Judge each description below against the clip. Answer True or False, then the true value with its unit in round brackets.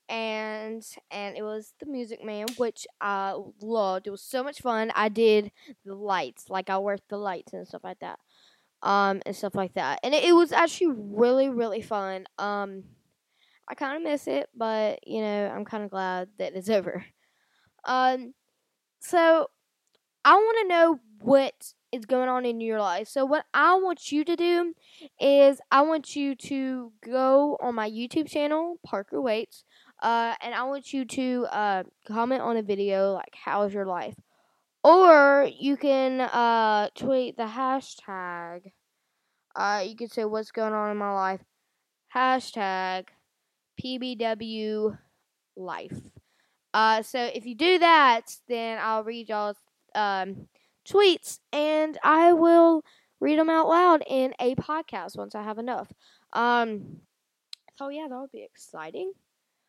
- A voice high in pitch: True (235 Hz)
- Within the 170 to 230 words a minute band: False (160 wpm)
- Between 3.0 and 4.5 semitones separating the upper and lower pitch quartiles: False (5.2 semitones)